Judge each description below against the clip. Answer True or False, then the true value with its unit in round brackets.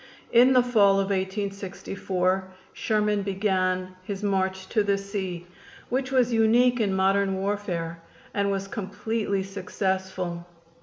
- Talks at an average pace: False (120 wpm)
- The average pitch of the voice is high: True (195 Hz)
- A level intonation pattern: True (1.9 semitones)